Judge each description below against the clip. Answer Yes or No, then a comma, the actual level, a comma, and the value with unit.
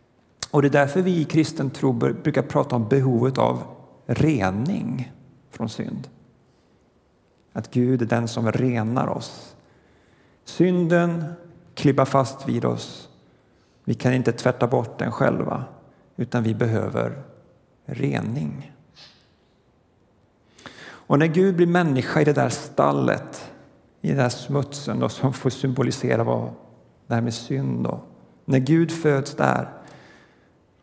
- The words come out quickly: No, slow, 125 wpm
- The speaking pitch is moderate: No, low, 130 Hz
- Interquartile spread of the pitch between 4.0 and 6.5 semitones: Yes, average, 4.3 semitones